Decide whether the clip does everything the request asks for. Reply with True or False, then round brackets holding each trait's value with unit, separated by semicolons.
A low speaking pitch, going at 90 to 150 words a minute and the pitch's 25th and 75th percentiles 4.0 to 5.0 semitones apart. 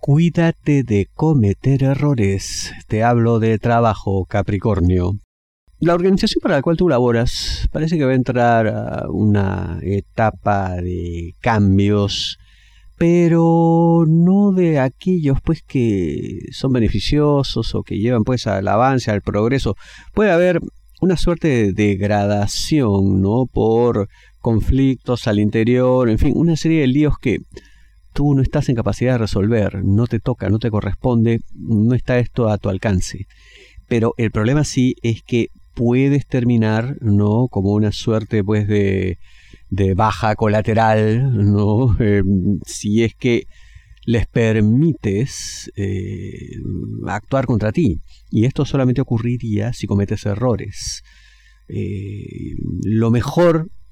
True (110 Hz; 130 wpm; 4.4 semitones)